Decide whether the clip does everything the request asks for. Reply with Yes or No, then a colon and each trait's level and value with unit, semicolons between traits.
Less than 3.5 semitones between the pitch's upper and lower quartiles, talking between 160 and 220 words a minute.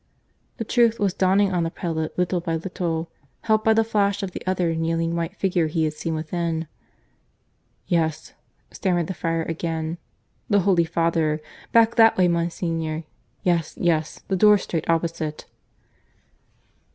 No: average, 2.7 semitones; average, 150 wpm